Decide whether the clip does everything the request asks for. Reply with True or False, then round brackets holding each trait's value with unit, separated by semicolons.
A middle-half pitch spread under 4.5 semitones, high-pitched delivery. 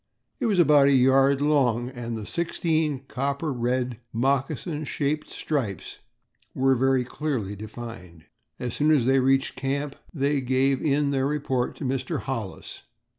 False (2.8 semitones; 135 Hz)